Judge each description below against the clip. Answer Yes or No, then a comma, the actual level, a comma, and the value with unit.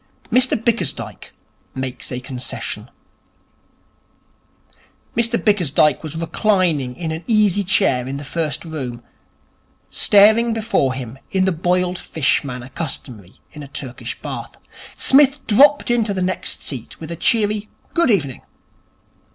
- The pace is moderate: No, slow, 125 wpm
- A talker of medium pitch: Yes, medium, 170 Hz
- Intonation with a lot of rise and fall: Yes, wide, 7.9 semitones